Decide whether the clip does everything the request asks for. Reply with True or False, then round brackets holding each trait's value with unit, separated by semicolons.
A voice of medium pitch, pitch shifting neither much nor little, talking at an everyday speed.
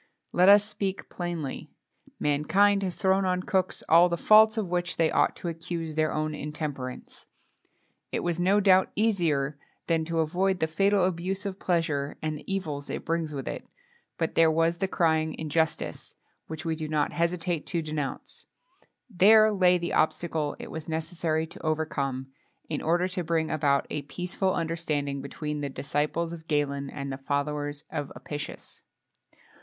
True (165 Hz; 3.2 semitones; 165 wpm)